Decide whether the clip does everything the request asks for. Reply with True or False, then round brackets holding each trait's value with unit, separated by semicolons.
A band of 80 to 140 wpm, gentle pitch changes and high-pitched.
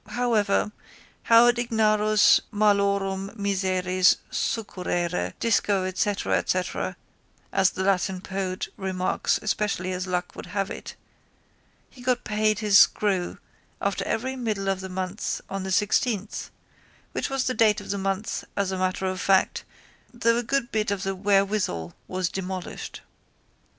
True (135 wpm; 2.3 semitones; 195 Hz)